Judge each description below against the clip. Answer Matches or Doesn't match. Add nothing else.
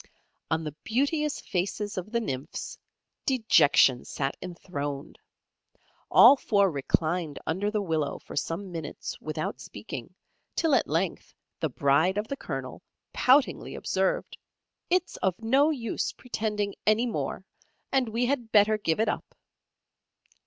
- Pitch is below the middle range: Doesn't match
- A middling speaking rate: Doesn't match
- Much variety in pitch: Matches